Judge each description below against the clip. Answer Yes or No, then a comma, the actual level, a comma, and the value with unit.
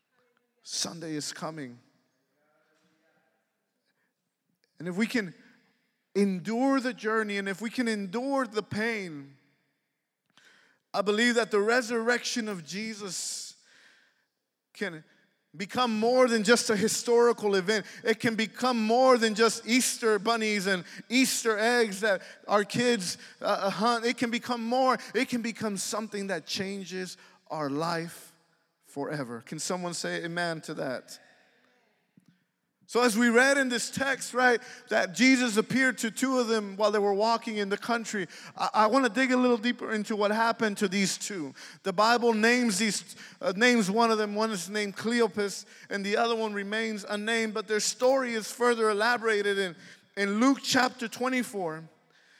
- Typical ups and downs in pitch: Yes, average, 3.4 semitones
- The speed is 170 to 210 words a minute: No, average, 150 wpm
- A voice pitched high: Yes, high, 220 Hz